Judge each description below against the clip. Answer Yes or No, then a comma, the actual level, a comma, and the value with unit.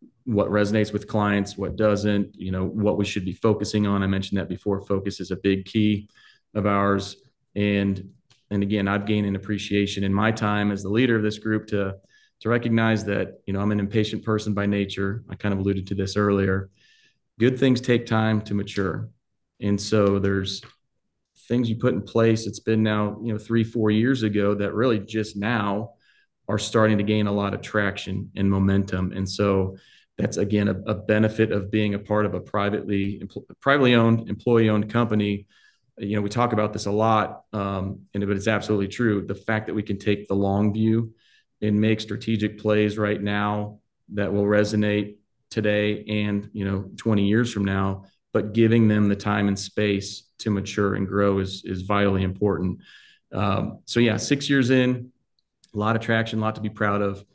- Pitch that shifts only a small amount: Yes, narrow, 1.5 semitones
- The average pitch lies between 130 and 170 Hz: No, low, 105 Hz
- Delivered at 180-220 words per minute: Yes, average, 200 wpm